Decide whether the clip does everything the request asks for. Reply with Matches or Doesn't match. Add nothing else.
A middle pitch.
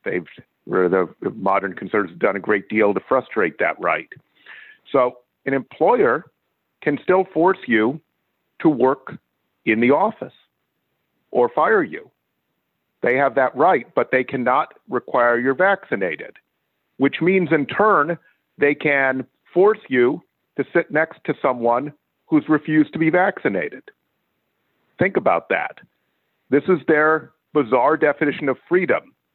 Matches